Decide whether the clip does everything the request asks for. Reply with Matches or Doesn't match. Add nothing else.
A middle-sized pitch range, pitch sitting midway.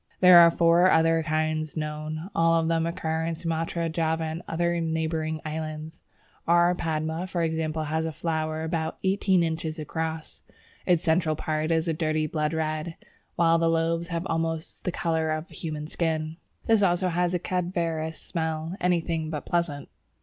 Doesn't match